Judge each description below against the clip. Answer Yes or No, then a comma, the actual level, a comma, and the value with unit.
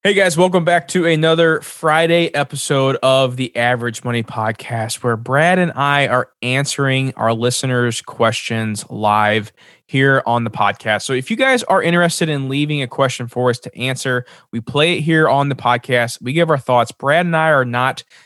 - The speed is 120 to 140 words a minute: No, average, 185 wpm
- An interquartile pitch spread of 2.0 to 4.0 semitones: No, average, 4.5 semitones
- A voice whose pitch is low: Yes, low, 130 Hz